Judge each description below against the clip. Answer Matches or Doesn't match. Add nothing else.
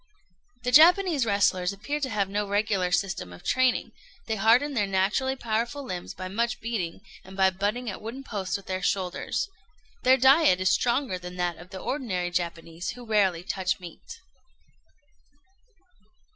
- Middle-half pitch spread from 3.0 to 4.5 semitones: Doesn't match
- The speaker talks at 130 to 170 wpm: Matches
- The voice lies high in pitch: Matches